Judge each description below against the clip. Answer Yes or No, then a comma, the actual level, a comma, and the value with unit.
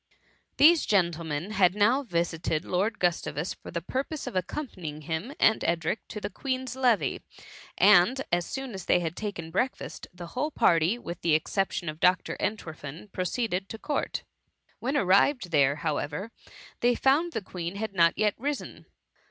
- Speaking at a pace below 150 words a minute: No, average, 160 wpm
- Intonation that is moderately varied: No, wide, 6.2 semitones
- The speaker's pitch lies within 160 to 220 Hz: Yes, high, 190 Hz